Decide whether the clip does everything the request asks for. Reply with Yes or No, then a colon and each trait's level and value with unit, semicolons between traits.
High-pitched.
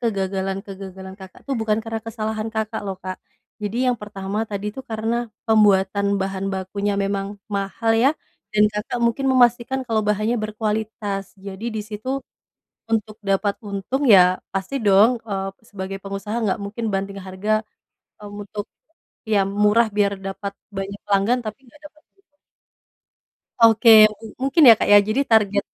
Yes: high, 210 Hz